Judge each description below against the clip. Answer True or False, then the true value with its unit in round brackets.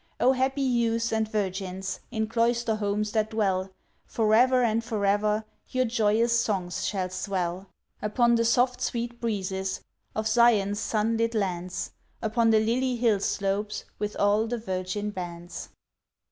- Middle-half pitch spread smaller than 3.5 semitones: True (2.9 semitones)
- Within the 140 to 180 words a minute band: True (145 wpm)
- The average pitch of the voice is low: False (215 Hz)